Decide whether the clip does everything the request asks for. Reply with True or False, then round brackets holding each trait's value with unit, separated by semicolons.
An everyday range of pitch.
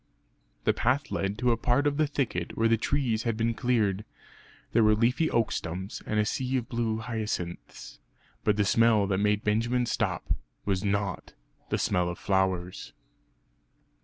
True (3.1 semitones)